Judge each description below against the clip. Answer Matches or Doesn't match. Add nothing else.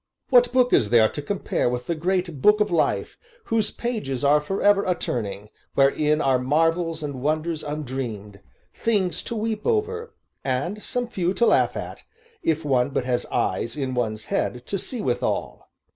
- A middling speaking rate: Matches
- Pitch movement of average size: Doesn't match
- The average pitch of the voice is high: Doesn't match